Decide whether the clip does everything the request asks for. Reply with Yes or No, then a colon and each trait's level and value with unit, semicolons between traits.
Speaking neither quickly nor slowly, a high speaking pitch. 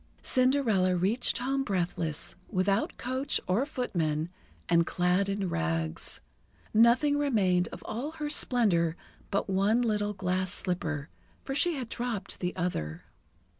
No: slow, 130 wpm; high, 195 Hz